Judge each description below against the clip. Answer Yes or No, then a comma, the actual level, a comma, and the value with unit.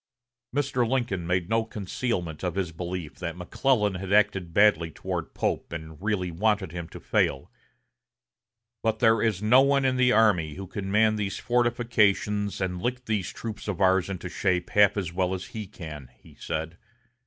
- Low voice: Yes, low, 100 Hz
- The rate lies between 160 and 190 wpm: Yes, average, 175 wpm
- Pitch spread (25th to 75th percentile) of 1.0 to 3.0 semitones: No, average, 3.9 semitones